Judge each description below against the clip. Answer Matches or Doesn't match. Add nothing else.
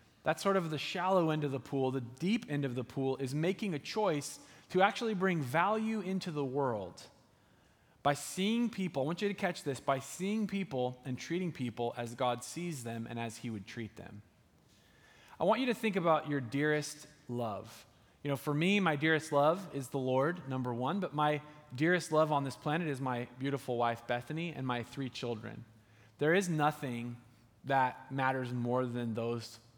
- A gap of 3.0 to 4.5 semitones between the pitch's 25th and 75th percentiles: Doesn't match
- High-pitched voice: Doesn't match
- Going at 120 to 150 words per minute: Doesn't match